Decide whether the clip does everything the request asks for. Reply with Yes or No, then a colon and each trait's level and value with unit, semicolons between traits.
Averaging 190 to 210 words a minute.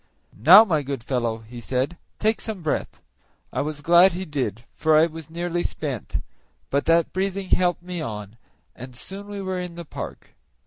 No: average, 180 wpm